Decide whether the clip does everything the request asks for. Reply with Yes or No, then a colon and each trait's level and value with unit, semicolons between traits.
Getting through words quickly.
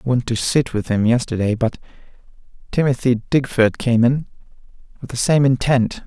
No: average, 160 wpm